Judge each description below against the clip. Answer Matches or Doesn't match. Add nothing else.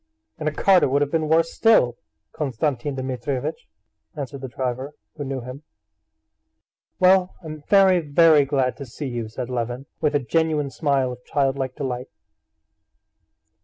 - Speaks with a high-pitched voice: Doesn't match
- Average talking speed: Matches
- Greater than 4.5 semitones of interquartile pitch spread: Doesn't match